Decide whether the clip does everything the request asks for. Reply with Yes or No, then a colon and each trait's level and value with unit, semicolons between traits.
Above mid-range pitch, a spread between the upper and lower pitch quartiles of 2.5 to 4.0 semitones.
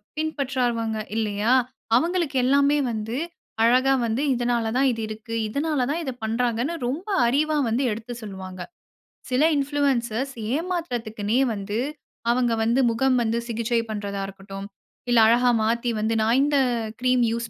Yes: high, 240 Hz; average, 3.6 semitones